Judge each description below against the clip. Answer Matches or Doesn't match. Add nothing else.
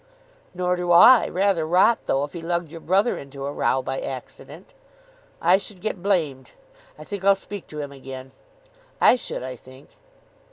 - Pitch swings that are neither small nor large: Doesn't match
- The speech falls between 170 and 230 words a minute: Matches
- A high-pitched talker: Doesn't match